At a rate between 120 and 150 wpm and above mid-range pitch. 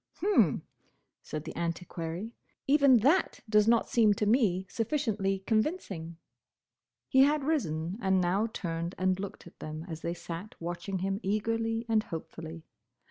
Yes: average, 140 wpm; high, 195 Hz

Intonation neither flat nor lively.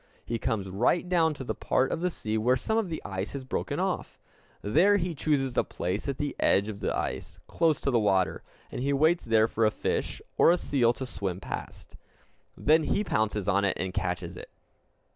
No: wide, 7.4 semitones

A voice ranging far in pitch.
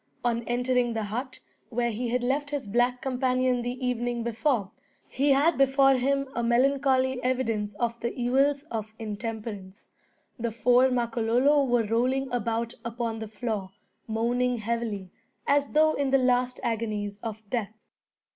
No: narrow, 2.5 semitones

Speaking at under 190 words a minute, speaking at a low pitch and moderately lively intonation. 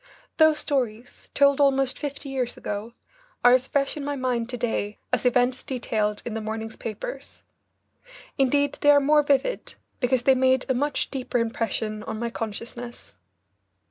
No: average, 160 wpm; very high, 255 Hz; average, 3.5 semitones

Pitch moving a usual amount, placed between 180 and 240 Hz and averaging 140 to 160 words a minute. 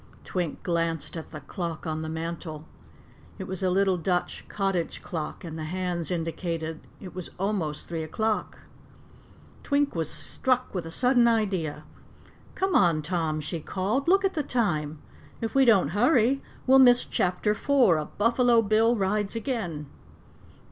No: wide, 5.9 semitones; medium, 185 Hz; average, 155 wpm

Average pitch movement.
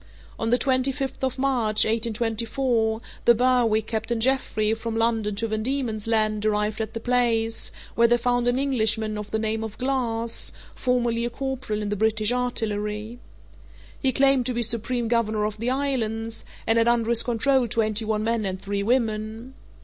No: narrow, 2.3 semitones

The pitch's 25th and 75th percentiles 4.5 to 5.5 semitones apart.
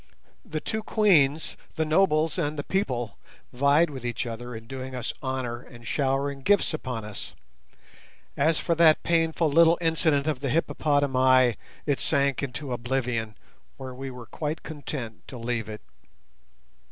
No: average, 4.1 semitones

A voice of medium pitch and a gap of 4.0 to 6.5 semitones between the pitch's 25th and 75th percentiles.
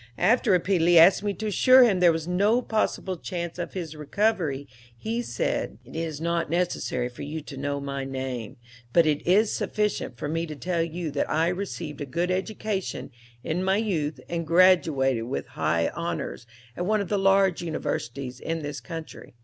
Yes: medium, 170 Hz; average, 4.6 semitones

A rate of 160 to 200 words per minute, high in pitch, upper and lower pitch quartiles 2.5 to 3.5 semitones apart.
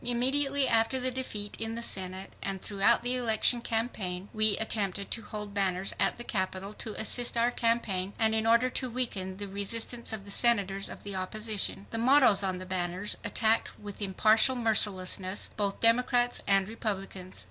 Yes: average, 170 wpm; high, 215 Hz; average, 3.2 semitones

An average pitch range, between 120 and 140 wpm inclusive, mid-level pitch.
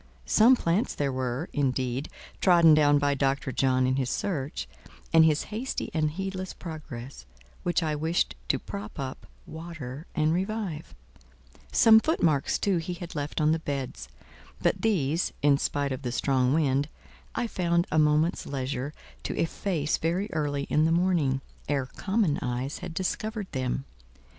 No: average, 4.2 semitones; average, 155 wpm; medium, 150 Hz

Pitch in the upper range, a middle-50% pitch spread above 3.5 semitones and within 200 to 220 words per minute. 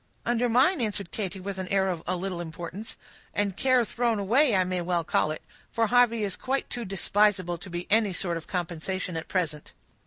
Yes: high, 195 Hz; average, 4.3 semitones; fast, 205 wpm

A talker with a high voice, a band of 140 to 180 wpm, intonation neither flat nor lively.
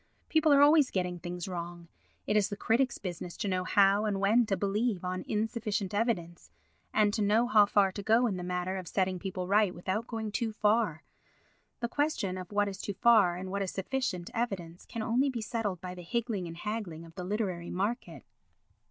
No: high, 200 Hz; fast, 205 wpm; average, 3.6 semitones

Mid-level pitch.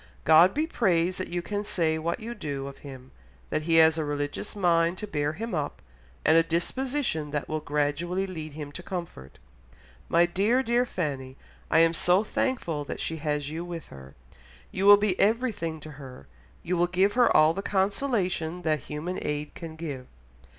Yes: medium, 165 Hz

